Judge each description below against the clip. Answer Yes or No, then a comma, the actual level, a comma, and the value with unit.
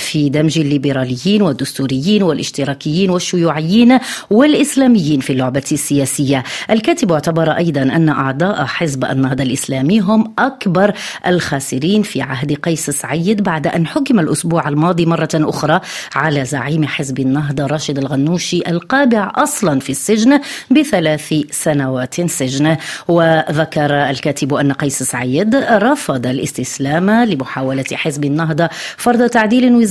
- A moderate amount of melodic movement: No, wide, 6.0 semitones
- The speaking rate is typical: Yes, average, 115 wpm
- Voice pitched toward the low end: No, medium, 155 Hz